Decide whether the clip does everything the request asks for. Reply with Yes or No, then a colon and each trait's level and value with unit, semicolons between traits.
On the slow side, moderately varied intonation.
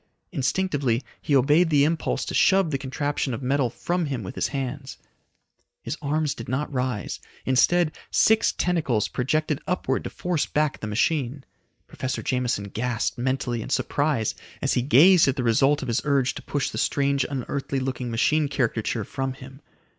No: average, 170 wpm; average, 3.0 semitones